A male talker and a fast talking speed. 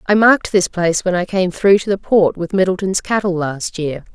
No: female; fast, 230 wpm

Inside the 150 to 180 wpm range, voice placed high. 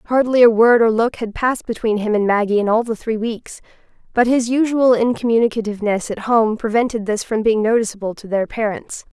No: average, 195 wpm; high, 225 Hz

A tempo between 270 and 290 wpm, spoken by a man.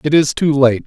Yes: fast, 275 wpm; male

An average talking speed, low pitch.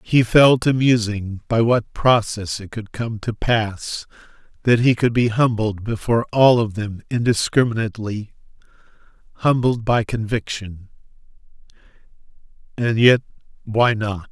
No: slow, 115 wpm; low, 115 Hz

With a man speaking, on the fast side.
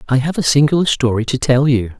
Yes: male; fast, 240 wpm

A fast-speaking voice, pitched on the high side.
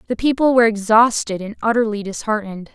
No: average, 155 wpm; high, 220 Hz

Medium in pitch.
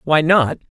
Yes: medium, 155 Hz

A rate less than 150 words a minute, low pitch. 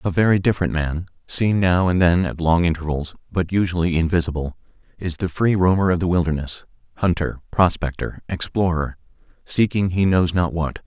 No: average, 155 wpm; very low, 85 Hz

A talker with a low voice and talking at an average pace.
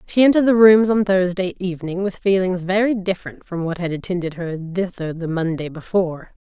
No: medium, 185 Hz; average, 185 wpm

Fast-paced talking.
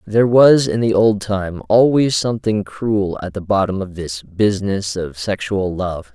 No: average, 175 wpm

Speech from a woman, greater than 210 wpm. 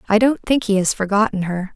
Yes: female; fast, 240 wpm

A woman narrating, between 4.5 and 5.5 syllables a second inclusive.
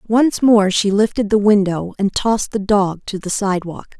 Yes: female; 4.8 syllables/s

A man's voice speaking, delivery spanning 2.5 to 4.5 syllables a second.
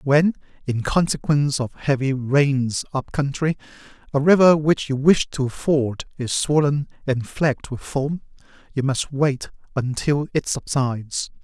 Yes: male; 4.1 syllables/s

